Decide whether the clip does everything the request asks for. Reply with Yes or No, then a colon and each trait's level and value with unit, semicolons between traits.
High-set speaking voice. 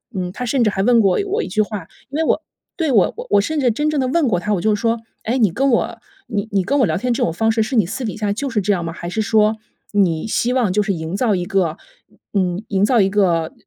Yes: high, 210 Hz